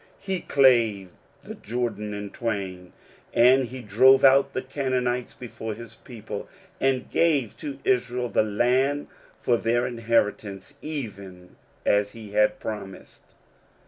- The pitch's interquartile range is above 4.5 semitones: No, average, 4.0 semitones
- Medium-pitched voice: No, low, 120 Hz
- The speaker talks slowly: Yes, slow, 125 wpm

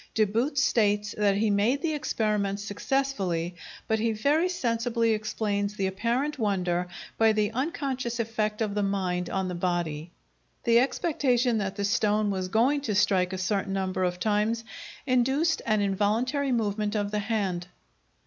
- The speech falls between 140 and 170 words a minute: Yes, average, 160 wpm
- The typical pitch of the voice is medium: No, high, 215 Hz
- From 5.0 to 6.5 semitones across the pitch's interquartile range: No, average, 3.4 semitones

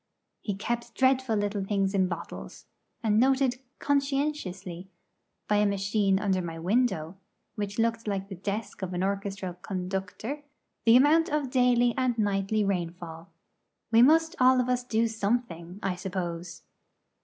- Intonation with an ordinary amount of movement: Yes, average, 4.7 semitones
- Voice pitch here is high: Yes, high, 205 Hz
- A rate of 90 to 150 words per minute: Yes, average, 145 wpm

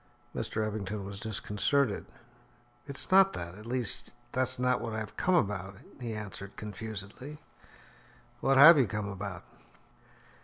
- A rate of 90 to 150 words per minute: Yes, average, 140 wpm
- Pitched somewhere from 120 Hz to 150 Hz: No, low, 110 Hz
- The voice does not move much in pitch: No, average, 4.3 semitones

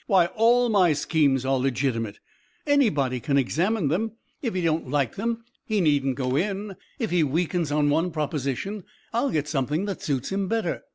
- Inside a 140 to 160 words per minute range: No, average, 175 wpm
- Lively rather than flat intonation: Yes, wide, 6.5 semitones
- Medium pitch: Yes, medium, 160 Hz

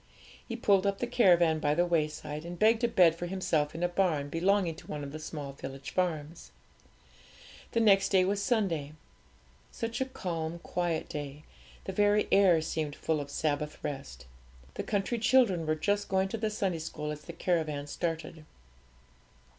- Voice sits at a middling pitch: Yes, medium, 170 Hz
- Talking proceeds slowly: No, average, 175 wpm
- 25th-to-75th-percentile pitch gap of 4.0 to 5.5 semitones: Yes, average, 4.5 semitones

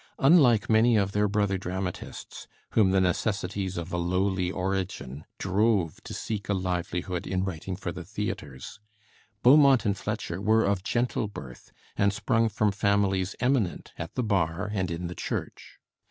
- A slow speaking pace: No, average, 155 wpm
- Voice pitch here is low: Yes, very low, 95 Hz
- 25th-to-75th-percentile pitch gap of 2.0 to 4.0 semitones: Yes, average, 2.8 semitones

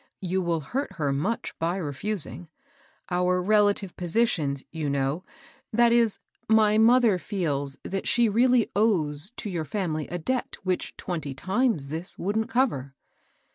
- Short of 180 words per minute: Yes, average, 145 wpm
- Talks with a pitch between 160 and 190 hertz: Yes, medium, 185 Hz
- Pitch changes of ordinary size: No, wide, 6.0 semitones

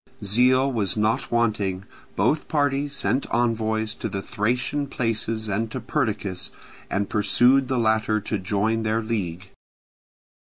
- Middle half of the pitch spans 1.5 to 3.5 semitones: Yes, average, 3.0 semitones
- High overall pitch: No, low, 110 Hz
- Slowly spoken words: Yes, slow, 130 wpm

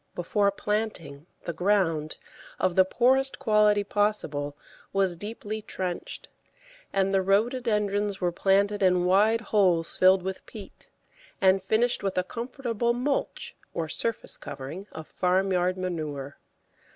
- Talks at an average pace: No, slow, 125 wpm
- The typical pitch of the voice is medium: No, high, 195 Hz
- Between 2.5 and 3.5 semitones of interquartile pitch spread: Yes, average, 2.9 semitones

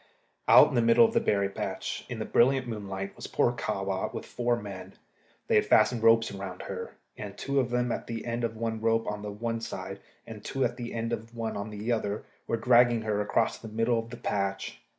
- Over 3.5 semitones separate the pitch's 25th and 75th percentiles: No, narrow, 2.4 semitones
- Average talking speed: No, fast, 225 wpm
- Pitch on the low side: Yes, low, 115 Hz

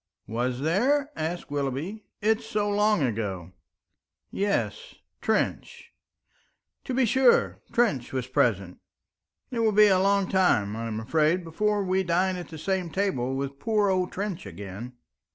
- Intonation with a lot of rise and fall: Yes, wide, 8.1 semitones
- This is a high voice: No, medium, 180 Hz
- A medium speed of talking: Yes, average, 145 wpm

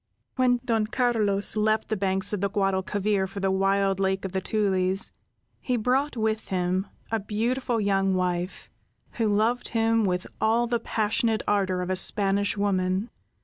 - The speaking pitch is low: No, high, 205 Hz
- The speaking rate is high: No, average, 160 wpm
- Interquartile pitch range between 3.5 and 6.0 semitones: No, average, 2.7 semitones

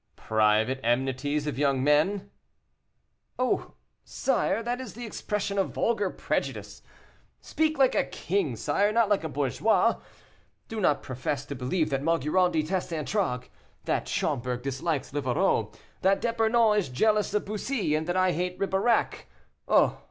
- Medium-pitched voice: Yes, medium, 175 Hz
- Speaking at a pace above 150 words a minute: No, average, 145 wpm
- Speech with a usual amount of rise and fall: No, wide, 7.3 semitones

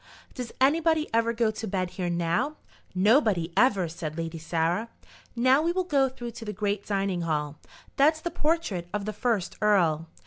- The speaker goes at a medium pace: Yes, average, 175 wpm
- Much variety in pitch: Yes, wide, 7.0 semitones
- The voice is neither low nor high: No, high, 210 Hz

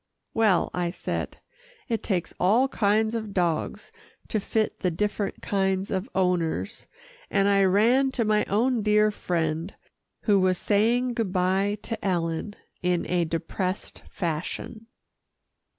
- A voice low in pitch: No, high, 200 Hz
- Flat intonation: No, average, 3.2 semitones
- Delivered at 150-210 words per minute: No, slow, 135 wpm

